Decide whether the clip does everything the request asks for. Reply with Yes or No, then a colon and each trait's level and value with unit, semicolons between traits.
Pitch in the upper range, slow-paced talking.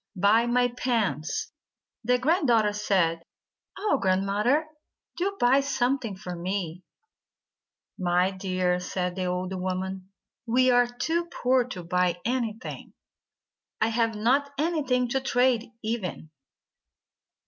Yes: high, 225 Hz; slow, 125 wpm